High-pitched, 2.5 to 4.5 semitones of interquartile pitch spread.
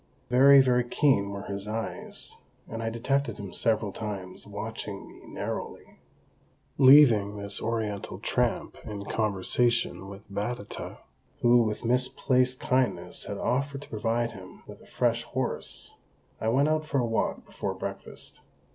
No: low, 115 Hz; average, 3.7 semitones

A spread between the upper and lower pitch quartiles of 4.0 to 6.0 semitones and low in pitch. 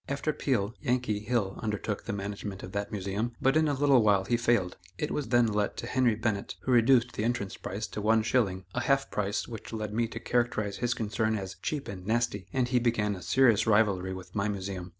No: average, 3.2 semitones; low, 110 Hz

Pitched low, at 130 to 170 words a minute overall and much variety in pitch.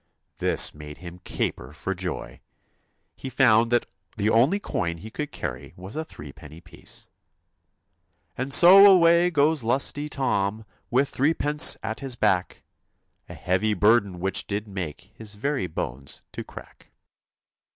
Yes: low, 110 Hz; average, 140 wpm; wide, 7.4 semitones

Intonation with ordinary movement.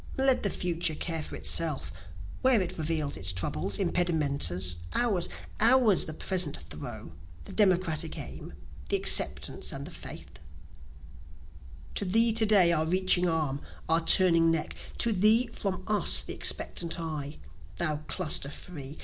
Yes: average, 4.5 semitones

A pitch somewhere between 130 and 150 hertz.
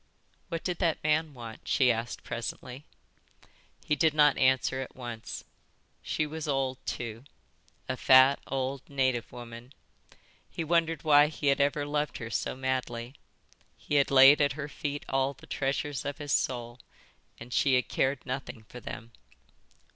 Yes: low, 135 Hz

